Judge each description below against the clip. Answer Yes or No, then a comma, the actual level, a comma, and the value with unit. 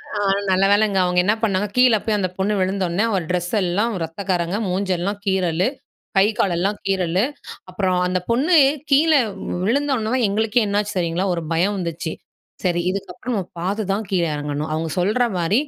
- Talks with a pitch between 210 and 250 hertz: No, high, 190 Hz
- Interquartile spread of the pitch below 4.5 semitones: Yes, average, 3.0 semitones